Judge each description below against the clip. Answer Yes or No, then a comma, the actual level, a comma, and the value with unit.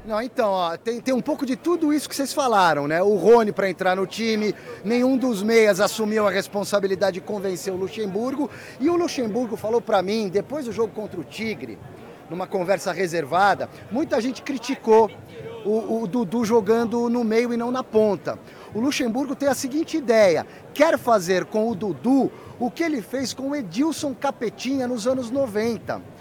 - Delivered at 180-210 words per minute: Yes, fast, 185 wpm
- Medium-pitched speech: No, high, 230 Hz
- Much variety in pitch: No, average, 4.4 semitones